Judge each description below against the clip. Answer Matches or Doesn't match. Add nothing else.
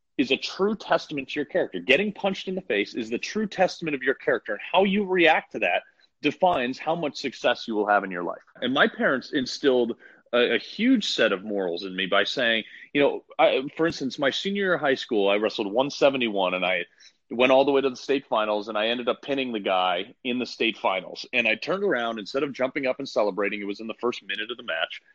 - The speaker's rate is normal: Doesn't match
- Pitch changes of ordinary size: Doesn't match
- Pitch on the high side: Doesn't match